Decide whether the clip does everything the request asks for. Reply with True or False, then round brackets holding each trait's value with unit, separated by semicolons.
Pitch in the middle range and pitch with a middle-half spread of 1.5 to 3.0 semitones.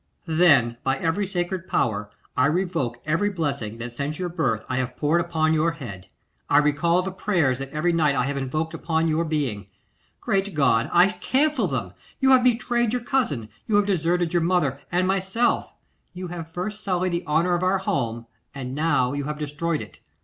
False (165 Hz; 4.8 semitones)